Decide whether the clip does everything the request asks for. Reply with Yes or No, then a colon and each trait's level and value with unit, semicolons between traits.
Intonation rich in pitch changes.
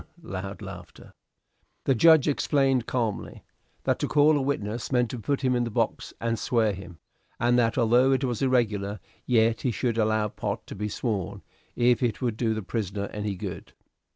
No: average, 3.2 semitones